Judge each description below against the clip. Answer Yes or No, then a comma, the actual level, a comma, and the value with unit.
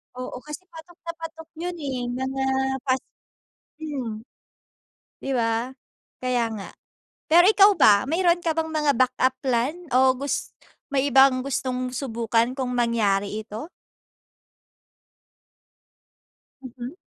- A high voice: Yes, very high, 260 Hz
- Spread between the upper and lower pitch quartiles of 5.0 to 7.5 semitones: No, average, 4.3 semitones